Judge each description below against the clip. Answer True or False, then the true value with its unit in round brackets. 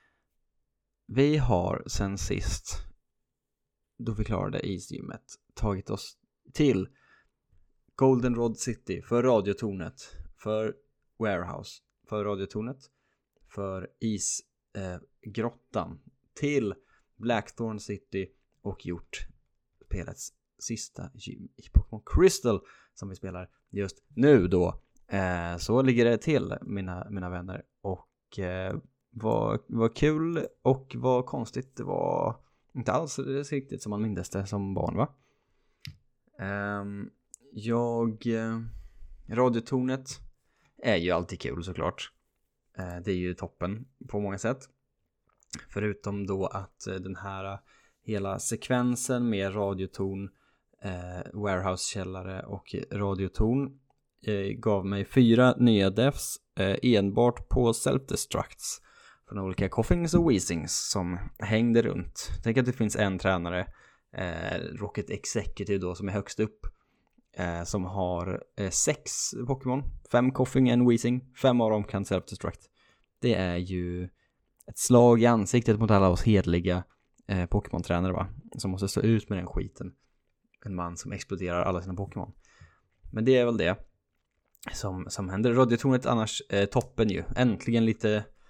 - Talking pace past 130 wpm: False (125 wpm)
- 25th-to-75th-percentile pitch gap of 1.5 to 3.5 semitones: False (4.2 semitones)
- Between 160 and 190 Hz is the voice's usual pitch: False (105 Hz)